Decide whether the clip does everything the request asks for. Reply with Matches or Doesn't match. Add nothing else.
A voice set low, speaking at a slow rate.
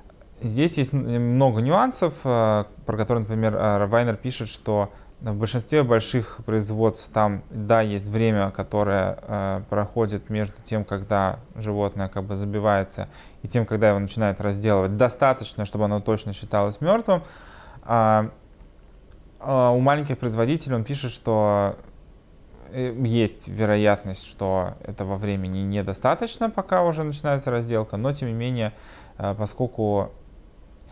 Doesn't match